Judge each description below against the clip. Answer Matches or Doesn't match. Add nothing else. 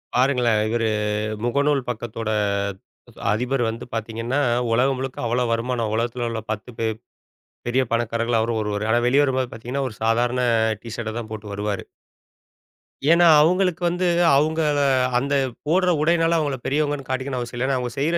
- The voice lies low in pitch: Matches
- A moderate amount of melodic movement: Matches